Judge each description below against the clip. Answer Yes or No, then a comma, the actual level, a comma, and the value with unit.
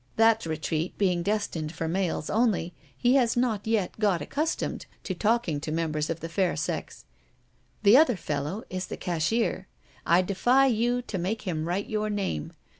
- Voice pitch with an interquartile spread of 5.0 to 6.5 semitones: Yes, wide, 5.4 semitones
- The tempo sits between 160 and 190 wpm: Yes, average, 170 wpm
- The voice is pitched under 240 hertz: Yes, high, 190 Hz